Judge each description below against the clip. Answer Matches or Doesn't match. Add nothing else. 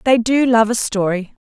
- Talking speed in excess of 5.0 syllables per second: Doesn't match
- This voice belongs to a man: Doesn't match